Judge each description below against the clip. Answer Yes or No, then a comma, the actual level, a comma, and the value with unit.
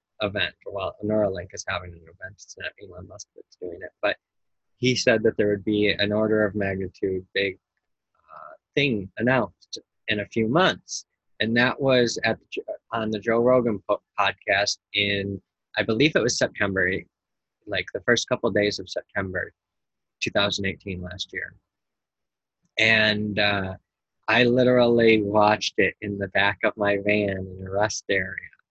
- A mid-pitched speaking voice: No, low, 105 Hz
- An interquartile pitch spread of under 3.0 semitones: Yes, narrow, 2.6 semitones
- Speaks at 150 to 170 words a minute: Yes, average, 165 wpm